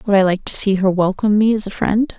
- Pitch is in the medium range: No, high, 200 Hz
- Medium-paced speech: No, fast, 300 wpm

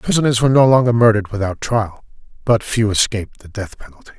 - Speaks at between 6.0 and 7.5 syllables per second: Yes, 6.5 syllables/s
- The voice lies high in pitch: No, low, 110 Hz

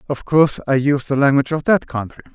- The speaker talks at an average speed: No, fast, 230 wpm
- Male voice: Yes, male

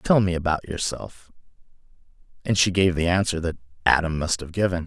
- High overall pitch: No, very low, 90 Hz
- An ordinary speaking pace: Yes, average, 175 wpm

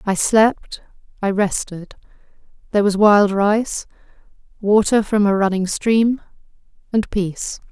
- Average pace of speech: No, slow, 110 wpm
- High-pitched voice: Yes, high, 205 Hz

